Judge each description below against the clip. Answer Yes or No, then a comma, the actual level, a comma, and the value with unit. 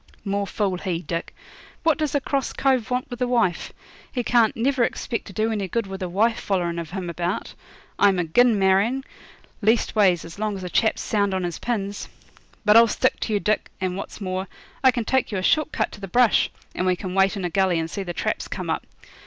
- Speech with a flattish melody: No, average, 4.1 semitones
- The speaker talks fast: Yes, fast, 225 wpm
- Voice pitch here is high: Yes, high, 200 Hz